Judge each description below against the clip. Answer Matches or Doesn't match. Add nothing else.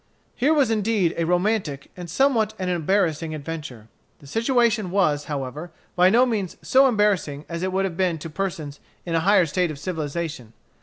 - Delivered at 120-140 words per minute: Doesn't match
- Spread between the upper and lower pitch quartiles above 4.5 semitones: Matches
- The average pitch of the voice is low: Doesn't match